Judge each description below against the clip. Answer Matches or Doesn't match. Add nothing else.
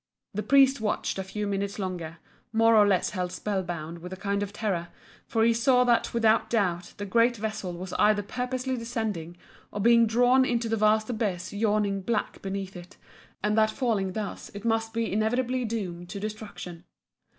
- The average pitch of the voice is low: Doesn't match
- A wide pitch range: Doesn't match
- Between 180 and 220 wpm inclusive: Matches